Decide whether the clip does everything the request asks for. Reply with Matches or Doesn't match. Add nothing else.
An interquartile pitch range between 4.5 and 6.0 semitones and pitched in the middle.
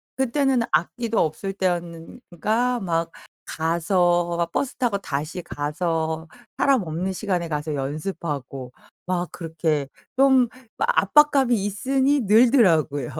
Doesn't match